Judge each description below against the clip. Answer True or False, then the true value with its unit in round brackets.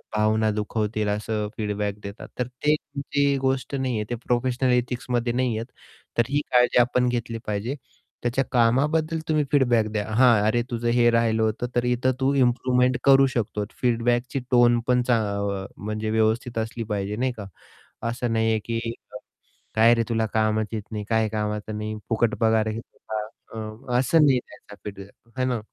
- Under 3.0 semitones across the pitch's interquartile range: True (2.5 semitones)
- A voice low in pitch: True (115 Hz)